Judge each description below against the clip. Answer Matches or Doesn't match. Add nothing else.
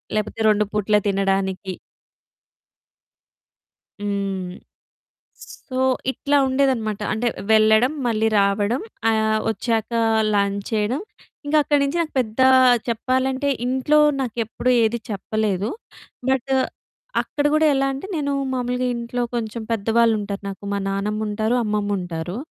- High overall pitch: Matches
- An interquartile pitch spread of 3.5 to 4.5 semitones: Matches